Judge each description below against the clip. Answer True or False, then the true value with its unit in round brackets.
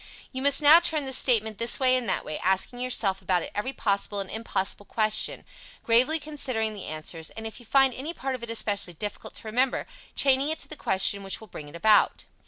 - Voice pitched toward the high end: True (225 Hz)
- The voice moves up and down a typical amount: True (4.9 semitones)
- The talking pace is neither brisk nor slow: False (220 wpm)